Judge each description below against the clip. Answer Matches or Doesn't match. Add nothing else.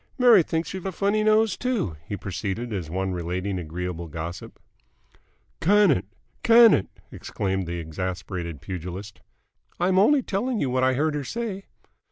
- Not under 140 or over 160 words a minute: Matches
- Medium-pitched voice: Doesn't match